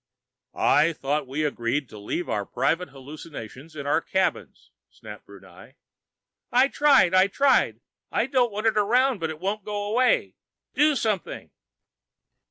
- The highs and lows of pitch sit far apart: Yes, wide, 7.5 semitones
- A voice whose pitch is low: No, medium, 185 Hz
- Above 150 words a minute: No, average, 145 wpm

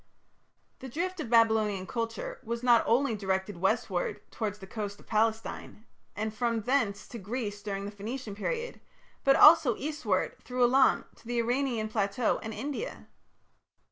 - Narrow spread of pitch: No, average, 3.5 semitones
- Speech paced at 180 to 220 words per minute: No, average, 155 wpm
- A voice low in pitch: No, high, 225 Hz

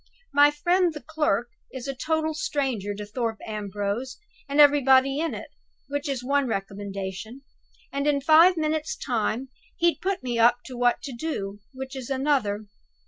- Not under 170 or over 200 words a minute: No, average, 160 wpm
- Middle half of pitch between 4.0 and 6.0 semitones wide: Yes, average, 4.8 semitones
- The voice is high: Yes, very high, 265 Hz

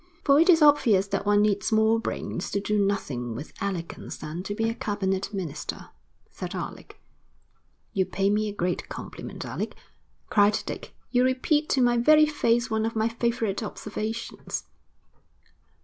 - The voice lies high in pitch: Yes, high, 215 Hz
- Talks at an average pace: Yes, average, 160 wpm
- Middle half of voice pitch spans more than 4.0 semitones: No, average, 3.2 semitones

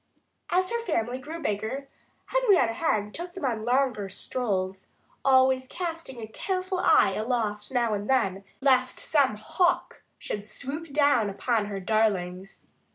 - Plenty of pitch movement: Yes, wide, 6.1 semitones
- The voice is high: Yes, very high, 250 Hz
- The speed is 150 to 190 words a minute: No, average, 140 wpm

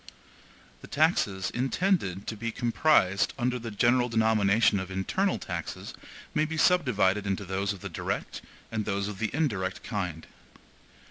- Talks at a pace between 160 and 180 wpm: No, average, 145 wpm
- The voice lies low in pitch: Yes, low, 110 Hz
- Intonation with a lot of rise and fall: No, average, 4.6 semitones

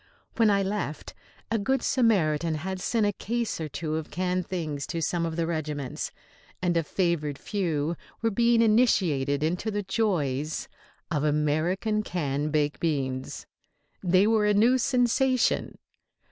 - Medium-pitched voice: Yes, medium, 175 Hz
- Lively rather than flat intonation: Yes, wide, 5.8 semitones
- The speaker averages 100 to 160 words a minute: Yes, average, 145 wpm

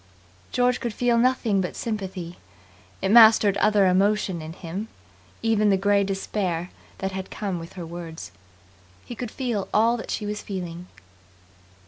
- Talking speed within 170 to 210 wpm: No, average, 145 wpm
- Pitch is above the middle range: Yes, high, 200 Hz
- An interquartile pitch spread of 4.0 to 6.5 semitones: No, average, 3.3 semitones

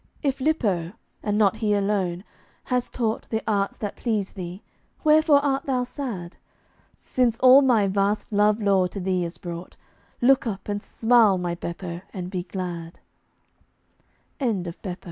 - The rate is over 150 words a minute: No, average, 145 wpm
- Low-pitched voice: No, high, 205 Hz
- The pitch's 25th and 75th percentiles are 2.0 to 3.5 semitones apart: No, average, 4.9 semitones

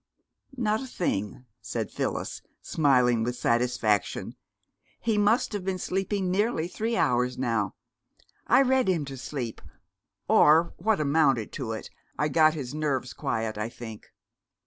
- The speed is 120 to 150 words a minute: Yes, average, 140 wpm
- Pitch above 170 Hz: No, medium, 145 Hz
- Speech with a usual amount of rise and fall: No, wide, 7.9 semitones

